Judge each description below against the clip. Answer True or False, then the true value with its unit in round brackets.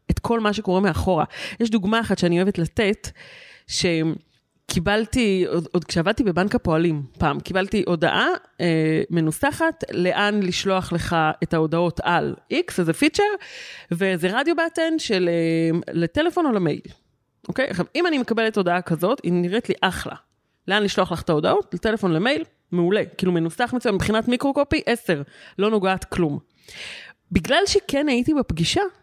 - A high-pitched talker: True (195 Hz)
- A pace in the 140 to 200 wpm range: True (150 wpm)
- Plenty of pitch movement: True (6.1 semitones)